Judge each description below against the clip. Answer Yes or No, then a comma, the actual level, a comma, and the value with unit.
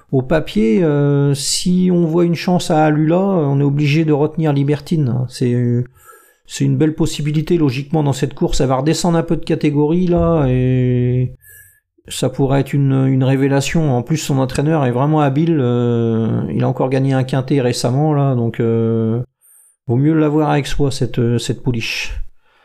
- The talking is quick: No, average, 175 wpm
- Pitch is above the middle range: No, medium, 145 Hz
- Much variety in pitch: No, average, 3.7 semitones